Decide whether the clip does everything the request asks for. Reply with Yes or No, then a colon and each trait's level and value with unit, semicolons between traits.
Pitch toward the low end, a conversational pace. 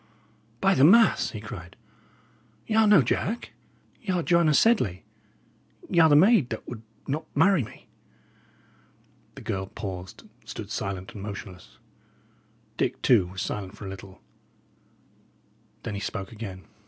Yes: low, 115 Hz; average, 145 wpm